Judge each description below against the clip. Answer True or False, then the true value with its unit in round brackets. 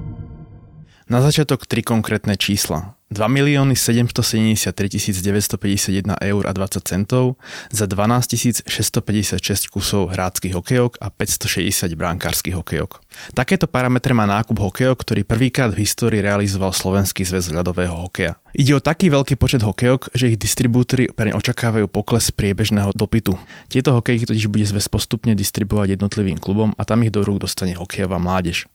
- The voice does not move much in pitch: False (3.7 semitones)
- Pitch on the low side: True (105 Hz)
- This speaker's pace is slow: False (140 wpm)